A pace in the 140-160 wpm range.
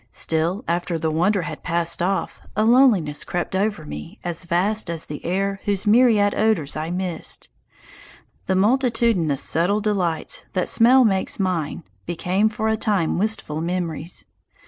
Yes: average, 145 wpm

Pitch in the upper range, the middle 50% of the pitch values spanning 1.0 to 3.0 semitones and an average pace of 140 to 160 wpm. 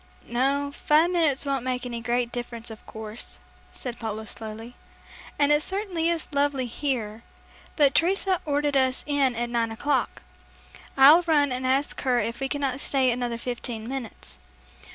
No: very high, 260 Hz; average, 3.4 semitones; average, 155 wpm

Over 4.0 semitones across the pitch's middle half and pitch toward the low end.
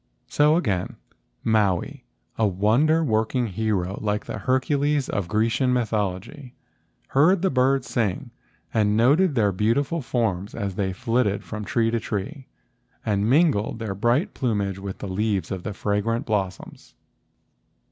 Yes: average, 4.5 semitones; low, 110 Hz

